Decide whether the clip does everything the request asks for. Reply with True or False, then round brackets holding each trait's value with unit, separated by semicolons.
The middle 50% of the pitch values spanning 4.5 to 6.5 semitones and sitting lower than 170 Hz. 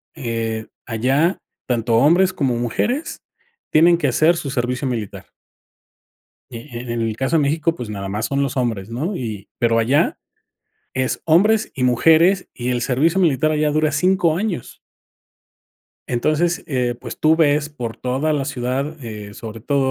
True (5.0 semitones; 135 Hz)